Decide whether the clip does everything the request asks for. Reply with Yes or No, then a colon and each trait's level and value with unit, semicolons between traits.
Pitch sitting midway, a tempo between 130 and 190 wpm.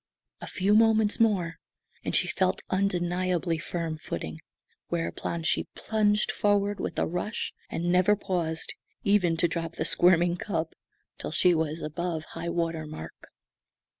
Yes: medium, 175 Hz; average, 140 wpm